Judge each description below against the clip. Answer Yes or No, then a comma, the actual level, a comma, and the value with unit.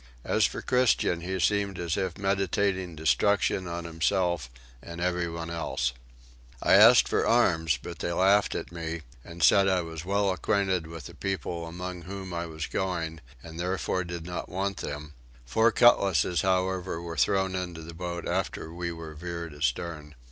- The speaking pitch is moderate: No, very low, 85 Hz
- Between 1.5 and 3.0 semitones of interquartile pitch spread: Yes, narrow, 2.4 semitones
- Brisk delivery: No, average, 165 wpm